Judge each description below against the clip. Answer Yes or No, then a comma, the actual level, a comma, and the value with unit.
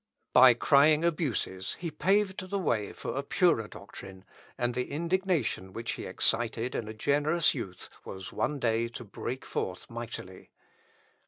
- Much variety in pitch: Yes, wide, 6.1 semitones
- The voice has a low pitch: Yes, low, 125 Hz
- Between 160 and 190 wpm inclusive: No, average, 150 wpm